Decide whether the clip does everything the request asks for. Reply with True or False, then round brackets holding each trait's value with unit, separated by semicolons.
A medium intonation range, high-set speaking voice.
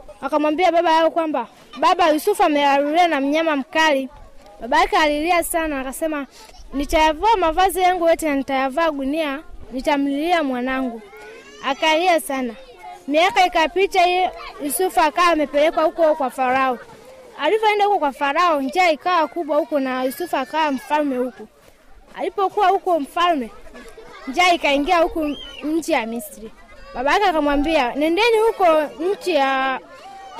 True (3.9 semitones; 315 Hz)